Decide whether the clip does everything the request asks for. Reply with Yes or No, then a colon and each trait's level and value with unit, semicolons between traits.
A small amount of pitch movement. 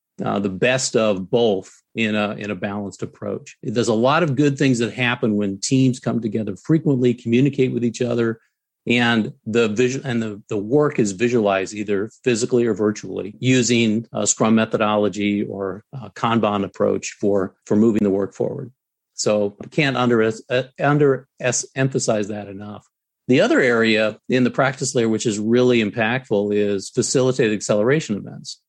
No: average, 3.2 semitones